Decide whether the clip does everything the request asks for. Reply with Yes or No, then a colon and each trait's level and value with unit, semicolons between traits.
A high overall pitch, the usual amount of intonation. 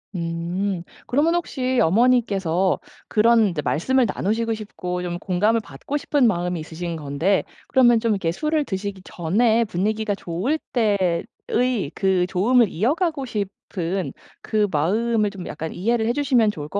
Yes: high, 205 Hz; average, 4.9 semitones